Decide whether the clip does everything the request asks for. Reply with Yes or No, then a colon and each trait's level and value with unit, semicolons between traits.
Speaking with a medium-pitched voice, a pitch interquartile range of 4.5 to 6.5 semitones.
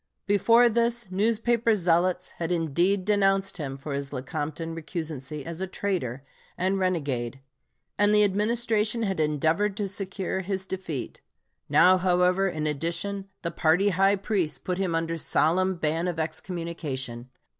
No: medium, 180 Hz; average, 3.9 semitones